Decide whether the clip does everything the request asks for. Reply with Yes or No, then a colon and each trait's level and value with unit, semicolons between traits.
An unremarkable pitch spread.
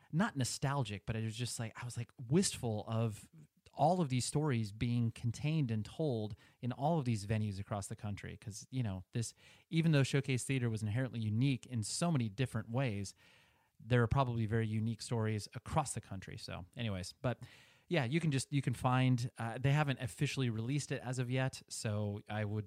Yes: average, 3.7 semitones